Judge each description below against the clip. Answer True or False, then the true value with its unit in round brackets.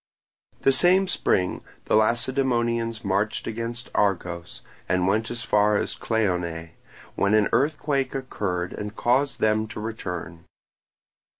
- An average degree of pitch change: True (3.9 semitones)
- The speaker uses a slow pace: True (120 wpm)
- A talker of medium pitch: False (110 Hz)